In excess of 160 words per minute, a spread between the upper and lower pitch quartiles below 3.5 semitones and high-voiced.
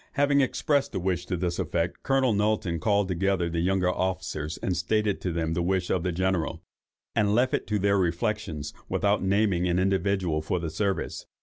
No: average, 185 wpm; average, 3.0 semitones; very low, 95 Hz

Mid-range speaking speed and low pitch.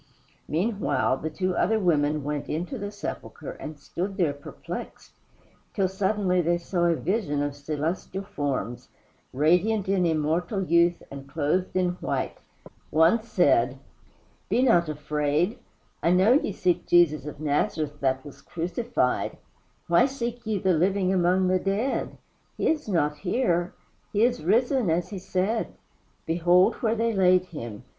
No: average, 145 wpm; medium, 175 Hz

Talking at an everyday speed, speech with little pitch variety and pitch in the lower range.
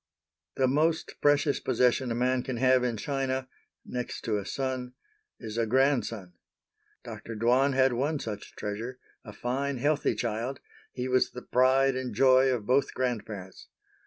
Yes: average, 155 wpm; narrow, 2.3 semitones; low, 130 Hz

